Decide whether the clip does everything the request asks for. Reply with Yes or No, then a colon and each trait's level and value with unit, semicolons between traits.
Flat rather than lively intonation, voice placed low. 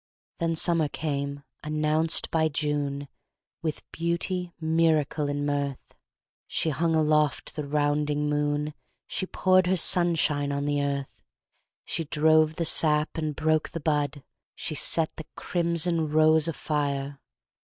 No: narrow, 1.9 semitones; medium, 150 Hz